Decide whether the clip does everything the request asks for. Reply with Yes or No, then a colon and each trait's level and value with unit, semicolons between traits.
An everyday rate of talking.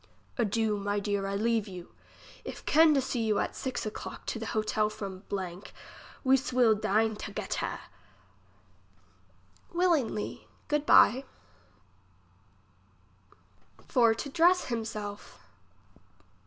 No: slow, 110 wpm